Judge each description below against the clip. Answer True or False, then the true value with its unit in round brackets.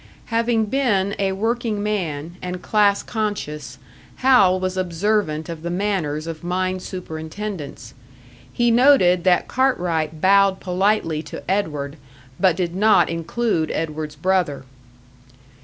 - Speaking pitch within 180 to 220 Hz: True (185 Hz)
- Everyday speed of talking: False (120 wpm)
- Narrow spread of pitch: False (4.4 semitones)